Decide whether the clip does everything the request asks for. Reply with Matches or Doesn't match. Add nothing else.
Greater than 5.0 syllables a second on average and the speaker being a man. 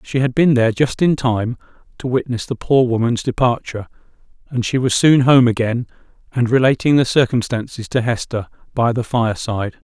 Matches